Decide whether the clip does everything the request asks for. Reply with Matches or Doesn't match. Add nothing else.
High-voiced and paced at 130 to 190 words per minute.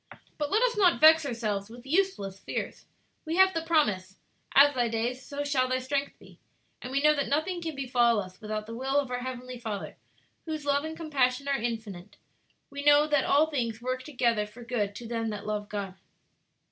Doesn't match